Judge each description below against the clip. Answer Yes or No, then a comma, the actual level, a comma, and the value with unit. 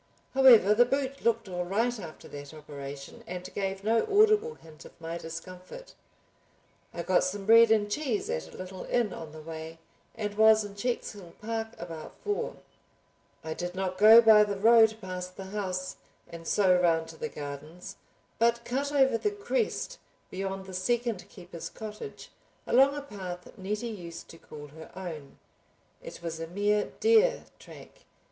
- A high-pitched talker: Yes, high, 195 Hz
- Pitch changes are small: No, average, 5.2 semitones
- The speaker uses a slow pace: No, average, 165 wpm